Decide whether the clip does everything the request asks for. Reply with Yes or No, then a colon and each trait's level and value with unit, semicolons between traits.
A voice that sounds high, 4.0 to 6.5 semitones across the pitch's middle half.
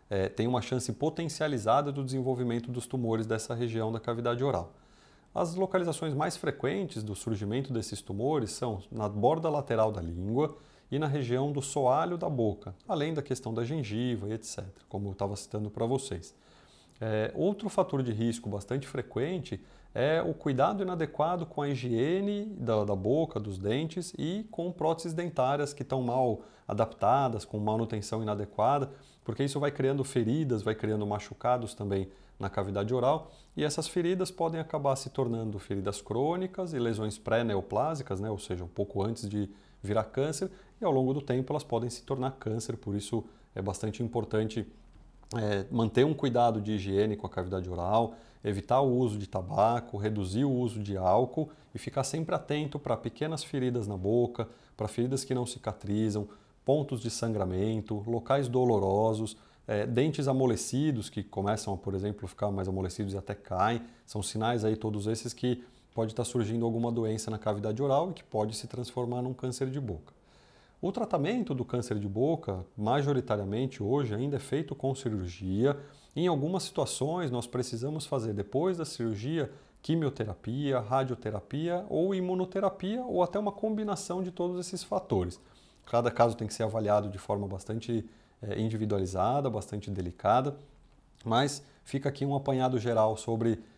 No: low, 120 Hz; average, 4.9 semitones